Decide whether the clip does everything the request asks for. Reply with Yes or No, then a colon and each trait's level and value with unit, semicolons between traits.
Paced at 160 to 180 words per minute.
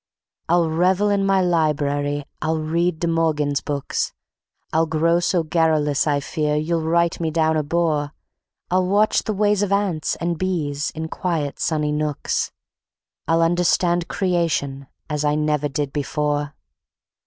No: average, 145 wpm